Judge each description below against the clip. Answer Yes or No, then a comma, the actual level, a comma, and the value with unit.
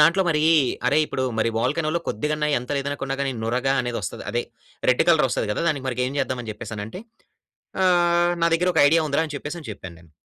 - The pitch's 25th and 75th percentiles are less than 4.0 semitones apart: No, average, 4.9 semitones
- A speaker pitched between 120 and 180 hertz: Yes, medium, 140 Hz